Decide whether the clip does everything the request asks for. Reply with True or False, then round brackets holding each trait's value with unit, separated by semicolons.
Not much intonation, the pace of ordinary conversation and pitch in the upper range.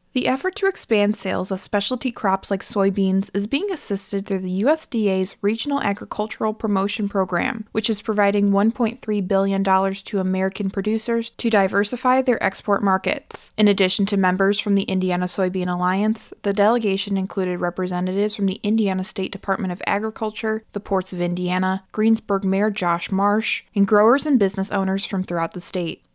True (2.3 semitones; 160 wpm; 200 Hz)